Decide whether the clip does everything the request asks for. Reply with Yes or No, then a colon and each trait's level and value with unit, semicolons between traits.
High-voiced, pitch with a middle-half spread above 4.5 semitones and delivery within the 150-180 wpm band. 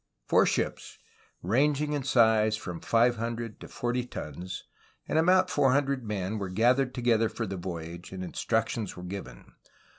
No: low, 115 Hz; average, 5.1 semitones; average, 155 wpm